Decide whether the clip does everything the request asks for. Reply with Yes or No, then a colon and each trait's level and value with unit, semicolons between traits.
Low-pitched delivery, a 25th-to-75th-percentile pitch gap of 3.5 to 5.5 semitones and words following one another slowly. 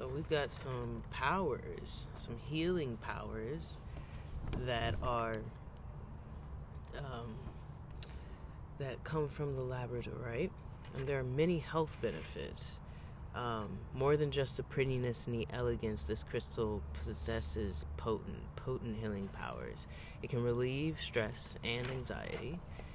Yes: low, 120 Hz; average, 3.9 semitones; slow, 120 wpm